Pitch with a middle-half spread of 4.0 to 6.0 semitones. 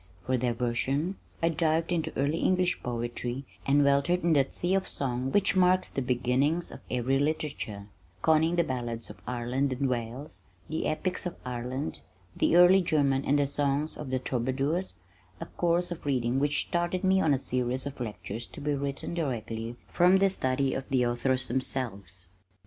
Yes: average, 4.7 semitones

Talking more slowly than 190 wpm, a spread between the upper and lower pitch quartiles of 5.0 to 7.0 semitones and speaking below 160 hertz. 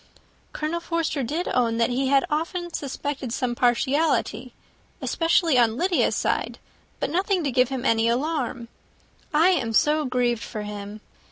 No: average, 150 wpm; average, 5.3 semitones; very high, 270 Hz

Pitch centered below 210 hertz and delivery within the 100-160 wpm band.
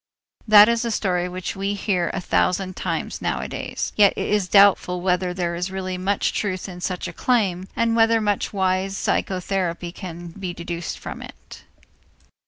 No: medium, 185 Hz; average, 170 wpm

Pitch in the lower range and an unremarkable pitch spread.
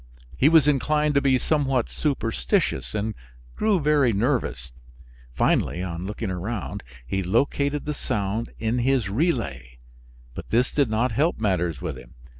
No: low, 115 Hz; wide, 6.8 semitones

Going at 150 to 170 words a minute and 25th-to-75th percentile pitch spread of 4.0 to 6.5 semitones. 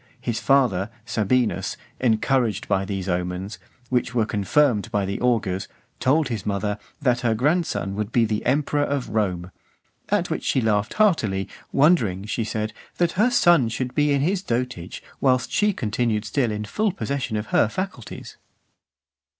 Yes: average, 155 wpm; average, 5.2 semitones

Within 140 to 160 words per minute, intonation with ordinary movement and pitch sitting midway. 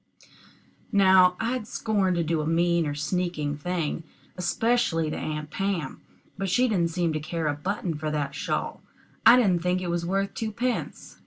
No: average, 170 wpm; average, 4.0 semitones; medium, 175 Hz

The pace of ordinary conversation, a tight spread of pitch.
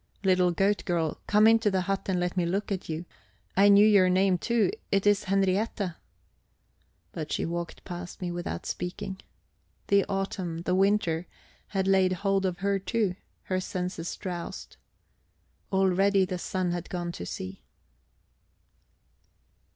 Yes: average, 145 wpm; narrow, 1.9 semitones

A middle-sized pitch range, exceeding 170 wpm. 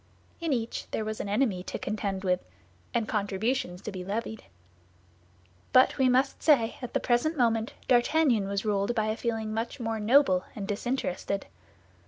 No: average, 3.6 semitones; average, 165 wpm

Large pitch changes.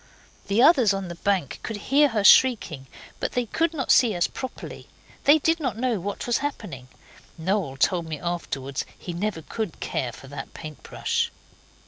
Yes: wide, 7.4 semitones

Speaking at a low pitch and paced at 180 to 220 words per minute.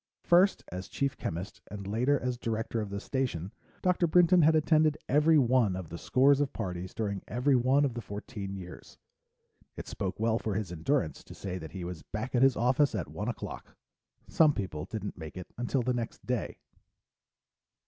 Yes: low, 115 Hz; average, 190 wpm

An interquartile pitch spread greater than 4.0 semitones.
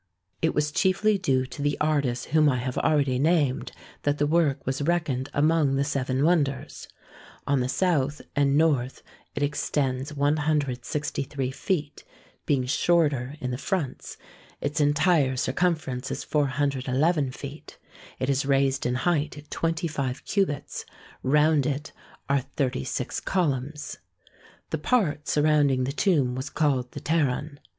No: average, 2.7 semitones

